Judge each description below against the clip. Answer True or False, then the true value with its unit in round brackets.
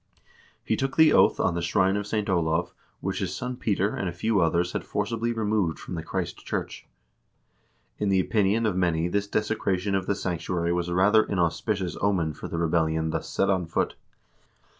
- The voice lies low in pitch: True (95 Hz)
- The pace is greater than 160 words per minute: True (190 wpm)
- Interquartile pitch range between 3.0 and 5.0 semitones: True (3.3 semitones)